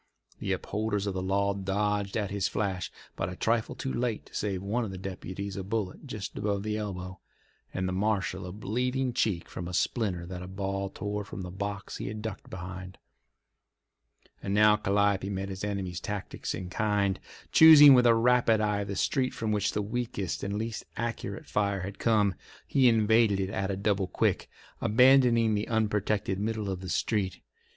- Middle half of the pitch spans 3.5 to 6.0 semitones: No, narrow, 2.4 semitones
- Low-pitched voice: Yes, low, 100 Hz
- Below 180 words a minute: No, average, 185 wpm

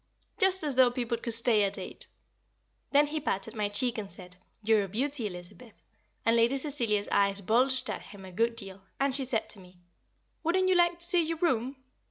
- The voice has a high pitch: Yes, high, 235 Hz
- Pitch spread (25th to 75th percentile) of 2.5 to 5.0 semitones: No, wide, 5.6 semitones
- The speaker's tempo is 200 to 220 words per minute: Yes, fast, 205 wpm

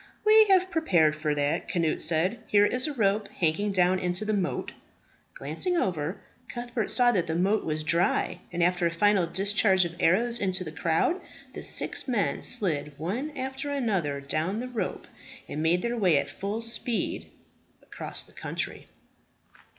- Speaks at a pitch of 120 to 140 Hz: No, high, 195 Hz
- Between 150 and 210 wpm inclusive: Yes, average, 165 wpm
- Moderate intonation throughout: No, wide, 6.1 semitones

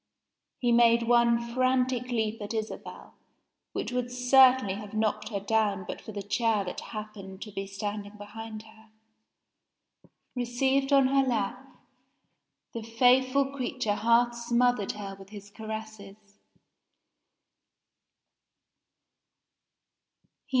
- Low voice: No, high, 225 Hz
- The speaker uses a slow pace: Yes, slow, 110 wpm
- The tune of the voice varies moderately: Yes, average, 3.1 semitones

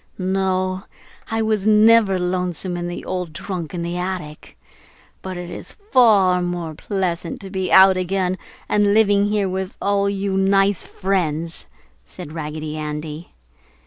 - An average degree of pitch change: No, narrow, 2.2 semitones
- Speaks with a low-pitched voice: No, medium, 185 Hz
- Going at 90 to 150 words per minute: Yes, average, 145 wpm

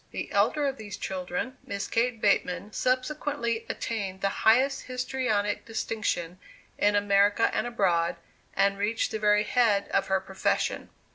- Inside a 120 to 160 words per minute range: Yes, average, 140 wpm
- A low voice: No, high, 210 Hz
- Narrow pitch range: No, average, 3.5 semitones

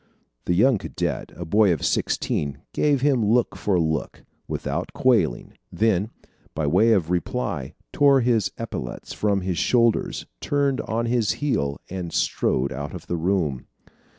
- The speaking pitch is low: Yes, low, 100 Hz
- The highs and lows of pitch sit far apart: Yes, wide, 6.4 semitones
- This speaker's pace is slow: No, average, 150 wpm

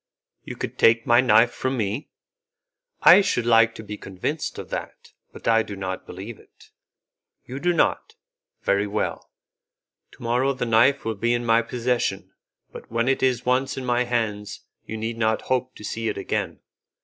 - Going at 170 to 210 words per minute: Yes, average, 180 wpm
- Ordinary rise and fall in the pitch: No, narrow, 2.3 semitones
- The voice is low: Yes, low, 115 Hz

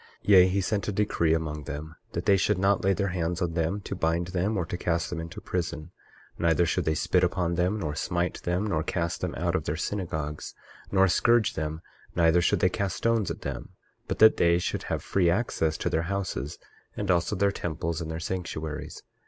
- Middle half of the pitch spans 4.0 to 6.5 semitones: No, average, 3.0 semitones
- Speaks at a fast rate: Yes, fast, 215 wpm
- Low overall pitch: Yes, very low, 85 Hz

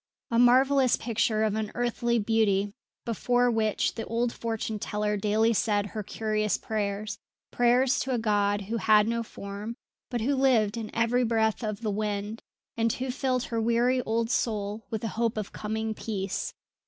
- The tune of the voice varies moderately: No, narrow, 2.1 semitones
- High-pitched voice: Yes, high, 225 Hz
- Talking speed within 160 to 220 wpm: Yes, average, 165 wpm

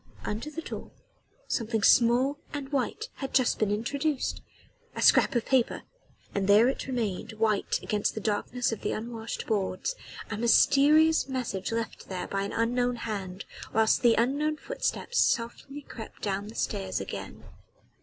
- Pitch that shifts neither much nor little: Yes, average, 4.2 semitones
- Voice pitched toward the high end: Yes, high, 230 Hz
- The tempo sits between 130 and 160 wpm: Yes, average, 155 wpm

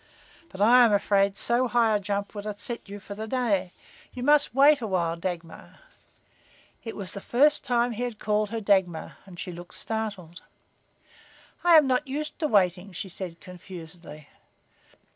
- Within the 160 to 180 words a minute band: Yes, average, 165 wpm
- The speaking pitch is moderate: No, high, 205 Hz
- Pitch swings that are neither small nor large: Yes, average, 4.7 semitones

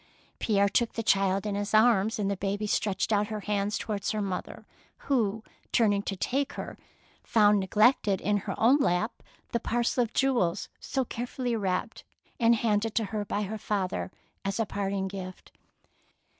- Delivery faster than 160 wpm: Yes, average, 170 wpm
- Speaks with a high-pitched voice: Yes, high, 210 Hz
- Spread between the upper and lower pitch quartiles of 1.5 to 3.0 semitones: Yes, narrow, 2.4 semitones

